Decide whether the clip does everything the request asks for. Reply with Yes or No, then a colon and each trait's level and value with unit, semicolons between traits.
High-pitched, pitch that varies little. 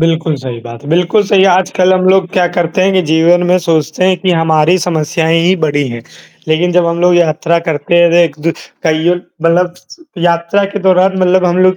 No: medium, 170 Hz; narrow, 2.2 semitones